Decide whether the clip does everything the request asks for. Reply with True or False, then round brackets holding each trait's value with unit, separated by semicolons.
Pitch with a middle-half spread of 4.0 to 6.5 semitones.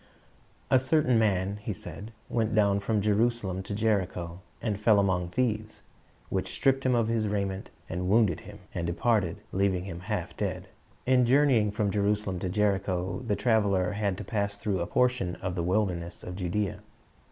False (3.1 semitones)